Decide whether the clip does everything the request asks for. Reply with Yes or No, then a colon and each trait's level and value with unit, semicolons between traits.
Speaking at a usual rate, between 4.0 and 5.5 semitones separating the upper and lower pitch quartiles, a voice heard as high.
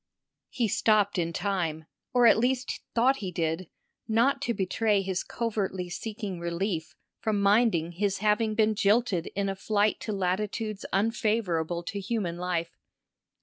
No: average, 145 wpm; average, 3.6 semitones; high, 200 Hz